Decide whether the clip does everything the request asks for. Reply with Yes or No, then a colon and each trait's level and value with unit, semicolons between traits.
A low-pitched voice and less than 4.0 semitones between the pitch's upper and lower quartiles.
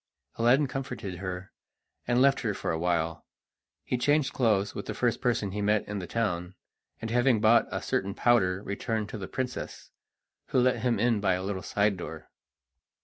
No: low, 105 Hz; average, 4.3 semitones